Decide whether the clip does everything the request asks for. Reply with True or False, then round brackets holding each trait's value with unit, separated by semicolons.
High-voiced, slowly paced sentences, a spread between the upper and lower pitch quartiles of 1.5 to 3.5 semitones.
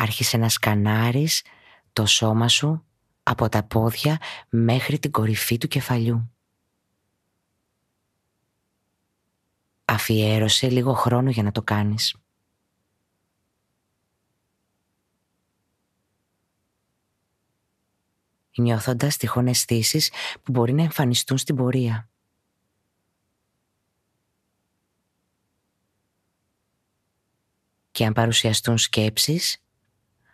False (110 Hz; 65 wpm; 3.2 semitones)